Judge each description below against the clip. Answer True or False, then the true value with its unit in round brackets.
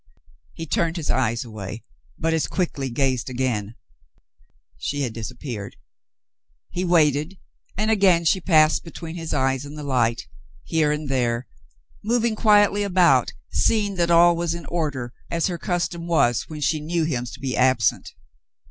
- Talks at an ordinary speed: True (155 wpm)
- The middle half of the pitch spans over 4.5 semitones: True (5.2 semitones)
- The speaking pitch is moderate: True (155 Hz)